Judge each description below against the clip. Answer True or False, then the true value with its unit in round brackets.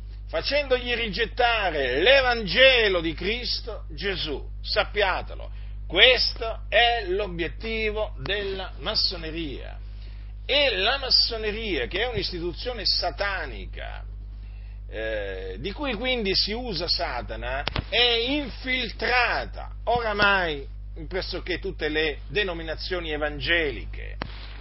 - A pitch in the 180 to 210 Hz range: True (190 Hz)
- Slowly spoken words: True (85 wpm)